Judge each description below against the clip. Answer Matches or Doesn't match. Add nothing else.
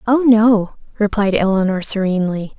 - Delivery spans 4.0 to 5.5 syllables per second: Matches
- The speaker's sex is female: Matches